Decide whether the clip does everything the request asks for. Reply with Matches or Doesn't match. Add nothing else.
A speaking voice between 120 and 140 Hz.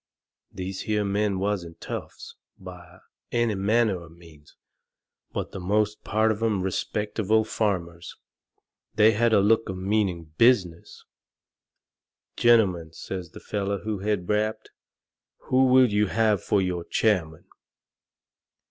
Doesn't match